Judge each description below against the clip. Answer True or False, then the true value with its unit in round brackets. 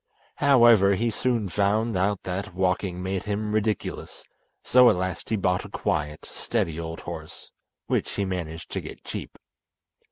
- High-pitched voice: False (100 Hz)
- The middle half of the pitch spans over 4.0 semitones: False (3.0 semitones)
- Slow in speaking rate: False (155 wpm)